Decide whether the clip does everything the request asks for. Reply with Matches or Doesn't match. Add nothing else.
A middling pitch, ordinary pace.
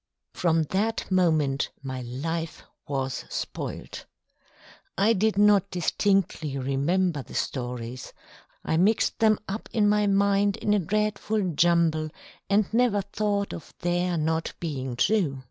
Doesn't match